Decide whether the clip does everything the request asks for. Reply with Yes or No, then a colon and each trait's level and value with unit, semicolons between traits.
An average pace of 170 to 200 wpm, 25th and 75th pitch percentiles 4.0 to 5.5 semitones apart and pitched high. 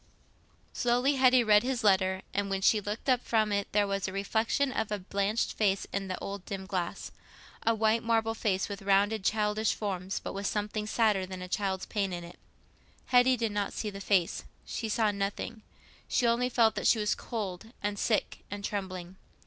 No: average, 190 wpm; narrow, 2.4 semitones; high, 205 Hz